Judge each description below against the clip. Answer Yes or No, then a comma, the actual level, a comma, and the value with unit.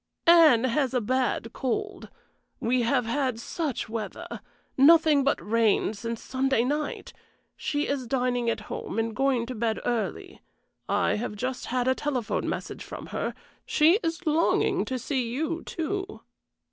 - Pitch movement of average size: Yes, average, 4.4 semitones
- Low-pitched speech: No, very high, 260 Hz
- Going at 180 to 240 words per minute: No, average, 150 wpm